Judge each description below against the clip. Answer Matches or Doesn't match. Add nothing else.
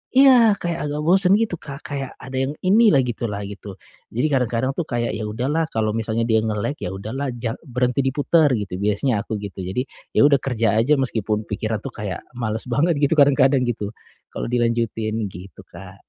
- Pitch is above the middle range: Doesn't match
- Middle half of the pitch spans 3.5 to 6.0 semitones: Matches